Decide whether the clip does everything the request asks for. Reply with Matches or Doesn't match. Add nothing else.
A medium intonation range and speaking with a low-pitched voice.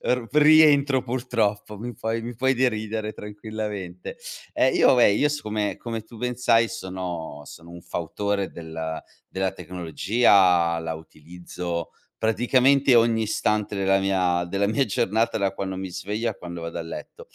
Matches